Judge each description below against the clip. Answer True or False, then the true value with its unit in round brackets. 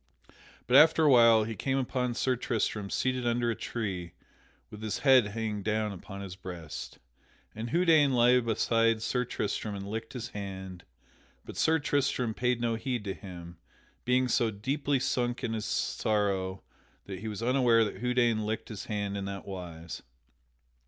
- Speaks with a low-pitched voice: True (115 Hz)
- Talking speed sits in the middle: True (165 wpm)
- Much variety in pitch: False (3.7 semitones)